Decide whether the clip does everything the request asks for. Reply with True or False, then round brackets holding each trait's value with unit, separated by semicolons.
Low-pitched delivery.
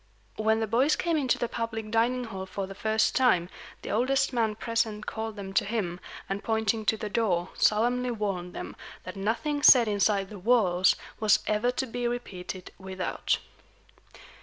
False (220 Hz)